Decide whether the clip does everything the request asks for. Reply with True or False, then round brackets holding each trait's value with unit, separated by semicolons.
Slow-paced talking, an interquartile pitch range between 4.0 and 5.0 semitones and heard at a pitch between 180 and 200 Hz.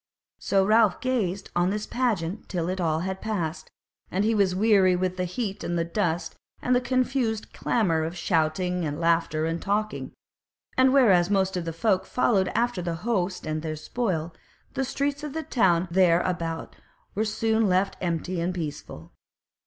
False (170 wpm; 4.5 semitones; 185 Hz)